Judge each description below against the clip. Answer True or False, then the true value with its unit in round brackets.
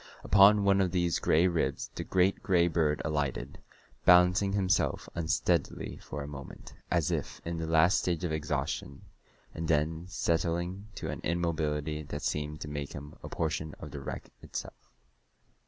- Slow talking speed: False (160 wpm)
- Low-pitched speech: True (80 Hz)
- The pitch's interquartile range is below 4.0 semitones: True (2.9 semitones)